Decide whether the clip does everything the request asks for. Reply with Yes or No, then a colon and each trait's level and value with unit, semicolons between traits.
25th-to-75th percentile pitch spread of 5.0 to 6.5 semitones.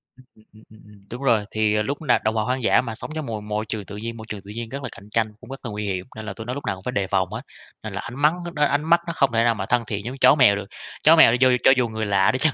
No: average, 3.7 semitones